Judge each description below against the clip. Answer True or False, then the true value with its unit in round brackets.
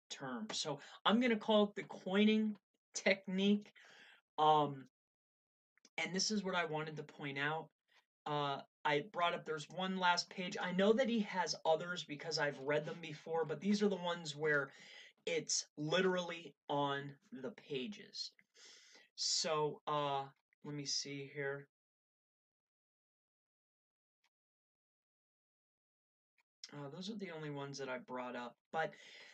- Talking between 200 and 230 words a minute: False (135 wpm)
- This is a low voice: False (160 Hz)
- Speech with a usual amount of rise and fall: False (6.0 semitones)